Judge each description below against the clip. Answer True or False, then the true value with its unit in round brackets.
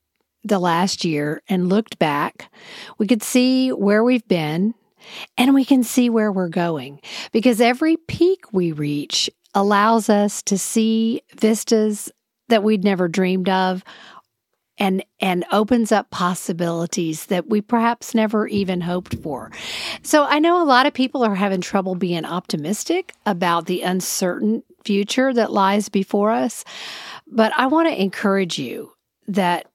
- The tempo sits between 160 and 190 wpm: False (145 wpm)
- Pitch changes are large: False (4.2 semitones)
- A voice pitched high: True (210 Hz)